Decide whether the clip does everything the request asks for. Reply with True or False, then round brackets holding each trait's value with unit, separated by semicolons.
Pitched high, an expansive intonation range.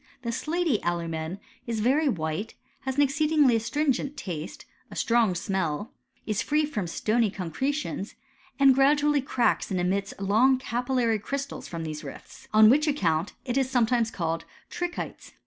True (230 Hz; 6.5 semitones)